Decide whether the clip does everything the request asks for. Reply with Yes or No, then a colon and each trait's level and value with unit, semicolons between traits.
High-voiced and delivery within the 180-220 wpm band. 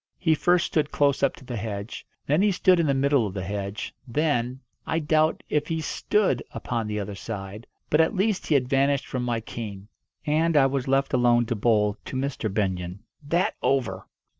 No: low, 130 Hz; average, 200 wpm